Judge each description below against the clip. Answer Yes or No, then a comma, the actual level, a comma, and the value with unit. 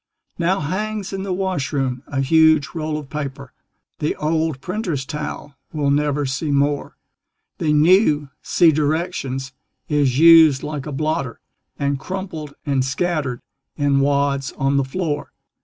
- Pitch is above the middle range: No, medium, 150 Hz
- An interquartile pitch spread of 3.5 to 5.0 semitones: No, average, 2.8 semitones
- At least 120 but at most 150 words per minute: Yes, average, 140 wpm